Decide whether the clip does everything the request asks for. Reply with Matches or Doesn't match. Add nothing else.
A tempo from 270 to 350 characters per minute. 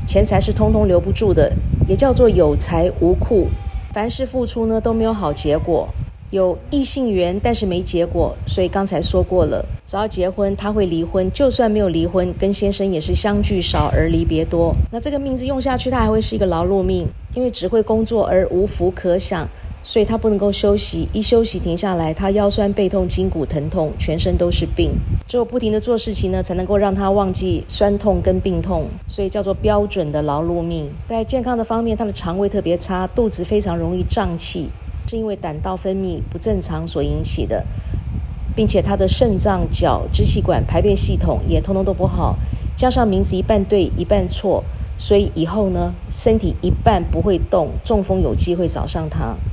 Matches